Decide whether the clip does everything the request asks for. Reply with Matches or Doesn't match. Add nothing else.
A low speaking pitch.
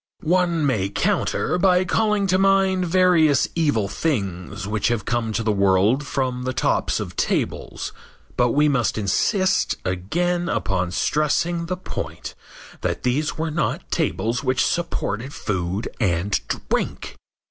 Matches